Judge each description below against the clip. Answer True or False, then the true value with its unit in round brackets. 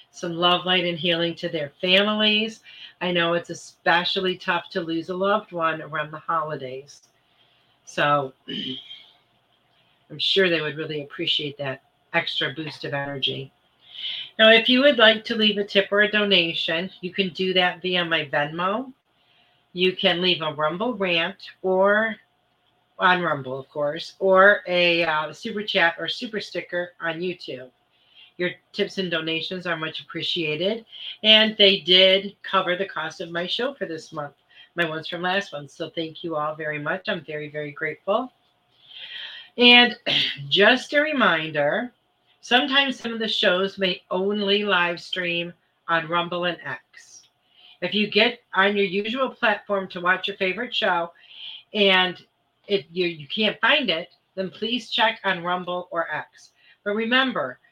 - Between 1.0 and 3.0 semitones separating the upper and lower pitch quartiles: False (4.1 semitones)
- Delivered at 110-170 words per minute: True (160 wpm)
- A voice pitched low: False (180 Hz)